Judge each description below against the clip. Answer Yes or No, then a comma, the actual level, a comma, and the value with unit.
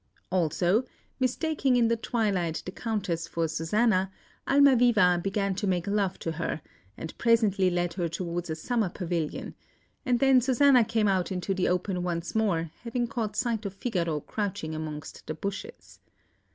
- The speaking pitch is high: Yes, high, 195 Hz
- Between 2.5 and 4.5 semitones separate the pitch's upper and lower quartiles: No, average, 4.9 semitones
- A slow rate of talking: No, average, 155 wpm